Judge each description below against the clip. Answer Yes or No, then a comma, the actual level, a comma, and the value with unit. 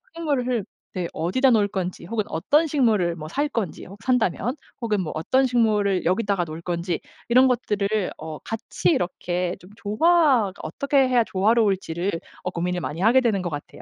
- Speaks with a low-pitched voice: No, high, 205 Hz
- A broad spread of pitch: Yes, wide, 5.7 semitones